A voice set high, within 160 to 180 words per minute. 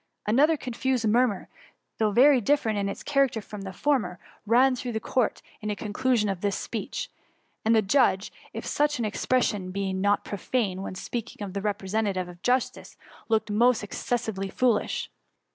Yes: high, 220 Hz; average, 170 wpm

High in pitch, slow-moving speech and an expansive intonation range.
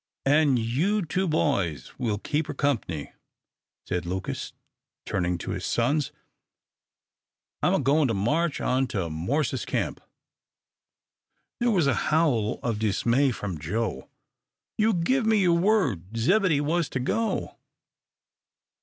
No: low, 135 Hz; slow, 130 wpm; wide, 8.1 semitones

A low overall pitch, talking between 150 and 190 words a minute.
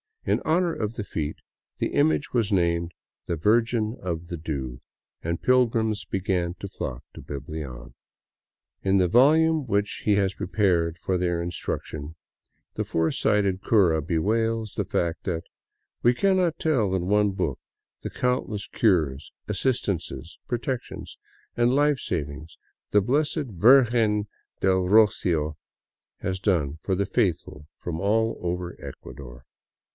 No: very low, 95 Hz; slow, 135 wpm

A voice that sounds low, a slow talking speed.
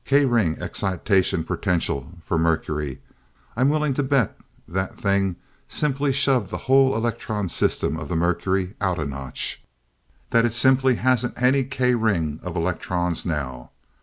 No: low, 100 Hz; average, 145 wpm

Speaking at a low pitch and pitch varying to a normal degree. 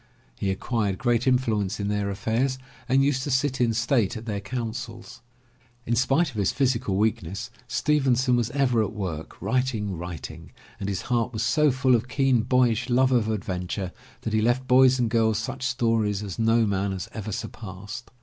Yes: low, 115 Hz; average, 3.7 semitones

